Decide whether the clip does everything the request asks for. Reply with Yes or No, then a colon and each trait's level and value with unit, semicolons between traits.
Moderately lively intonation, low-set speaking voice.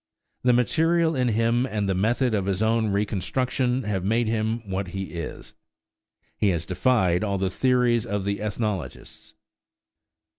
Yes: average, 4.0 semitones; low, 110 Hz